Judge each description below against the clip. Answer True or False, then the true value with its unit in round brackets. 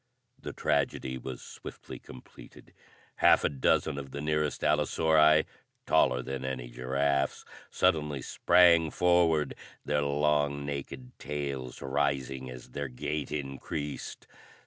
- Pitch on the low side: True (70 Hz)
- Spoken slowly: True (115 wpm)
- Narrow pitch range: True (2.1 semitones)